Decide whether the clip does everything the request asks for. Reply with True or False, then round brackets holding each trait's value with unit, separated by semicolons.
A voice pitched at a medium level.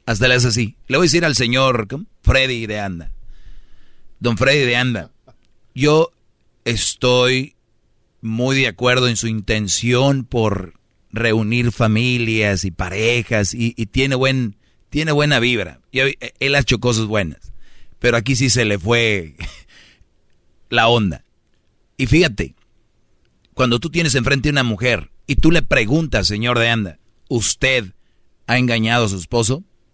False (120 Hz)